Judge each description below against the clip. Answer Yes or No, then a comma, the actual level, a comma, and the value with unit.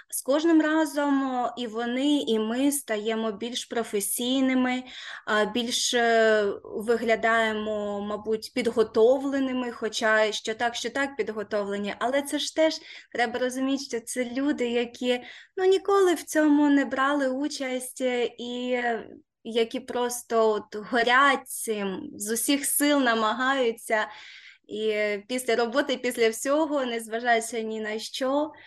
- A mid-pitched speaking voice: No, high, 245 Hz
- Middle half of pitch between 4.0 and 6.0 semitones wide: No, average, 3.6 semitones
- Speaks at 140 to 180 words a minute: No, average, 115 wpm